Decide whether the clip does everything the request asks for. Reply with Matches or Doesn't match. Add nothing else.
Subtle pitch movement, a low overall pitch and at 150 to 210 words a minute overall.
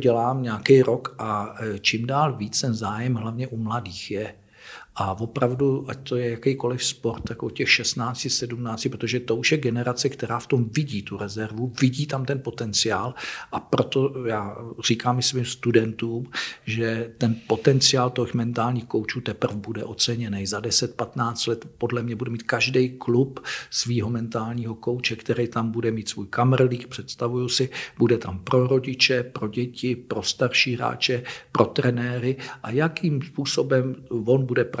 Matches